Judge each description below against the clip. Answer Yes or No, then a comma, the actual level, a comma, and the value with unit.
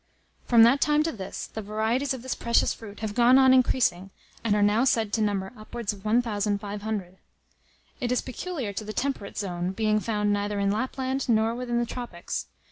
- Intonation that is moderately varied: Yes, average, 3.3 semitones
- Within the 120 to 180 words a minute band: No, average, 190 wpm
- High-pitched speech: Yes, high, 220 Hz